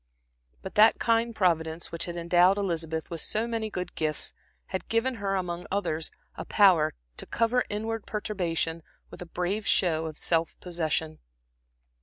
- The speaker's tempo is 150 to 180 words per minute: Yes, average, 155 wpm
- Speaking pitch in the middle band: Yes, medium, 180 Hz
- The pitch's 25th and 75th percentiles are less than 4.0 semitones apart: No, average, 4.4 semitones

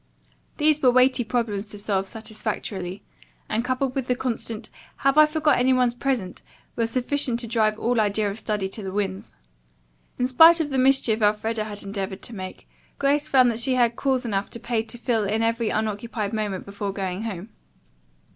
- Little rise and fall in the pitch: No, average, 3.5 semitones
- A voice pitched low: No, high, 225 Hz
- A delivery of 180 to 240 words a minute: Yes, average, 185 wpm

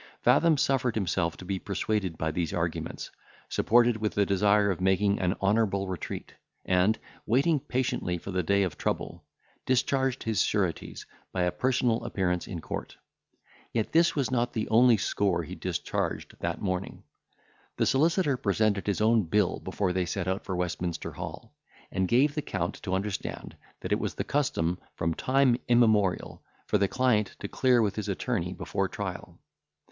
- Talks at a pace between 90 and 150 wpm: No, average, 165 wpm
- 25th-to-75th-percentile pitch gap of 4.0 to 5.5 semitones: Yes, average, 4.7 semitones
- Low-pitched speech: Yes, low, 100 Hz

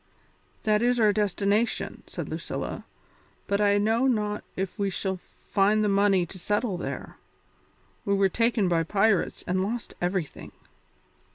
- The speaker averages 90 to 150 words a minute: Yes, average, 145 wpm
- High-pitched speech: Yes, high, 205 Hz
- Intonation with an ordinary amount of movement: No, narrow, 2.0 semitones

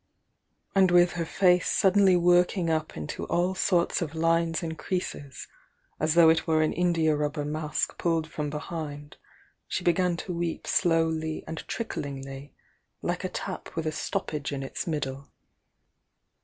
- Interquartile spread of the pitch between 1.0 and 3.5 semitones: Yes, narrow, 2.6 semitones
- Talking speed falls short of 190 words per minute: Yes, average, 150 wpm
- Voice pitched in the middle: Yes, medium, 160 Hz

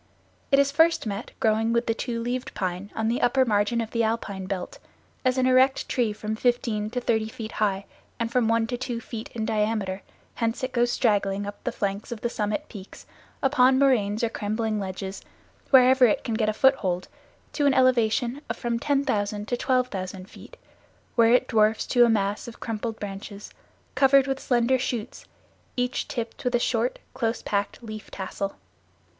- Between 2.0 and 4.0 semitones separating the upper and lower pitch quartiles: Yes, average, 3.1 semitones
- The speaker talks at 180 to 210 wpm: Yes, average, 185 wpm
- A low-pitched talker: No, high, 230 Hz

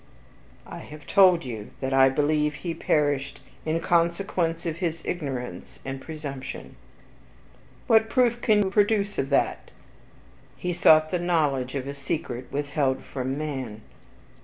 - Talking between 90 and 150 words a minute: Yes, slow, 135 wpm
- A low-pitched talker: No, medium, 150 Hz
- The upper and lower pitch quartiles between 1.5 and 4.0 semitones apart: No, average, 4.5 semitones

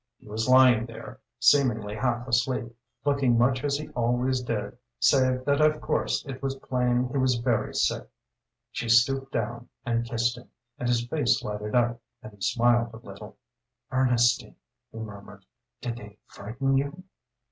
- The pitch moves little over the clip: Yes, narrow, 2.2 semitones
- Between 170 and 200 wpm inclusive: No, average, 160 wpm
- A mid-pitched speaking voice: No, low, 120 Hz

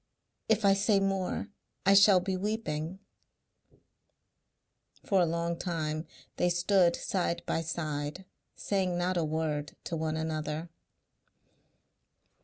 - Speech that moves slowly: Yes, slow, 115 wpm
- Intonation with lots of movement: No, average, 3.4 semitones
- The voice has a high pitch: No, medium, 175 Hz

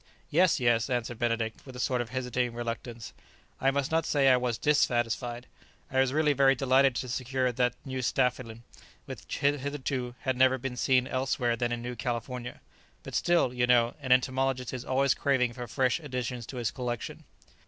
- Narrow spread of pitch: Yes, narrow, 1.7 semitones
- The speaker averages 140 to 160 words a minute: No, average, 180 wpm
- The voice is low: Yes, low, 125 Hz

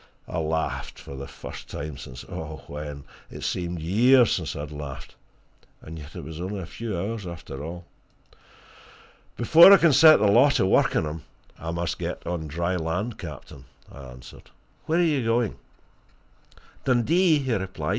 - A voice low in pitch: Yes, very low, 85 Hz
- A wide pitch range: Yes, wide, 7.2 semitones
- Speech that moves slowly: No, average, 170 wpm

